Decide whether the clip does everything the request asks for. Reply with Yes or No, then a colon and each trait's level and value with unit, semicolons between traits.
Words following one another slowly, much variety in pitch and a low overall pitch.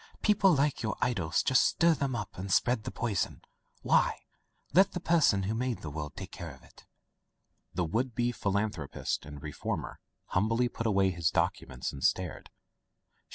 No: average, 170 wpm; wide, 6.1 semitones; low, 110 Hz